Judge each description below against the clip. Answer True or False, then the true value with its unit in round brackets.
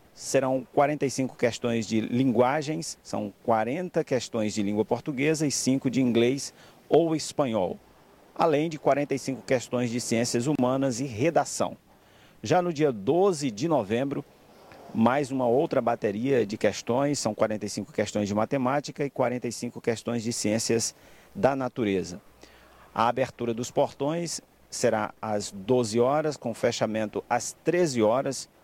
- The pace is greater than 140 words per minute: False (130 wpm)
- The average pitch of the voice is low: True (125 Hz)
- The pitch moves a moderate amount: True (3.8 semitones)